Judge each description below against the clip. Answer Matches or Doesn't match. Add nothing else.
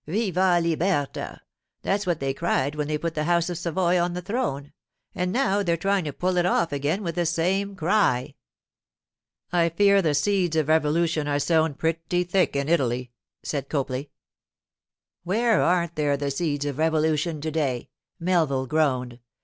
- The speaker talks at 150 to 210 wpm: Matches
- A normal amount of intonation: Matches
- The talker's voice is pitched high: Doesn't match